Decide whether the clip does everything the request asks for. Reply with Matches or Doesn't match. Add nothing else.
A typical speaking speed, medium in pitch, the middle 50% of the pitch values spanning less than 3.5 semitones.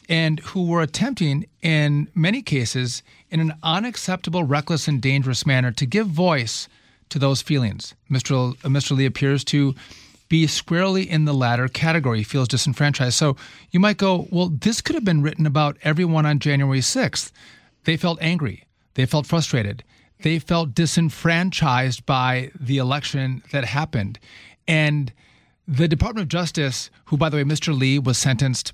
Doesn't match